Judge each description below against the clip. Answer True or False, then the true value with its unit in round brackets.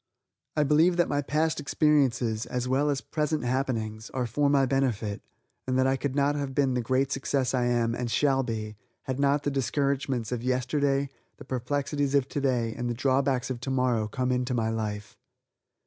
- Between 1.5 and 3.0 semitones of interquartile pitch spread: True (2.6 semitones)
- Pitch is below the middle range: True (130 Hz)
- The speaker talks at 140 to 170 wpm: False (185 wpm)